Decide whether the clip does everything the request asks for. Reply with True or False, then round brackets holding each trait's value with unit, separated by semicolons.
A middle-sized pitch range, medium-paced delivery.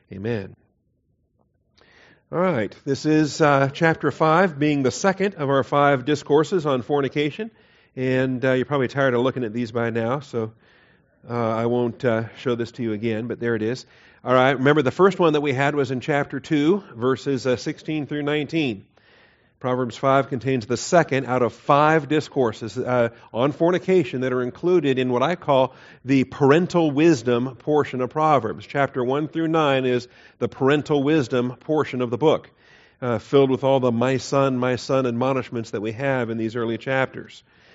True (3.3 semitones; 180 wpm)